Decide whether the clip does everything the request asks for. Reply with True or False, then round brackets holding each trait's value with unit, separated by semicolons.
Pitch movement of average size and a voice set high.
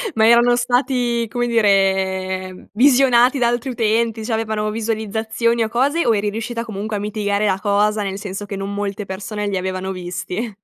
True (3.0 semitones; 215 Hz)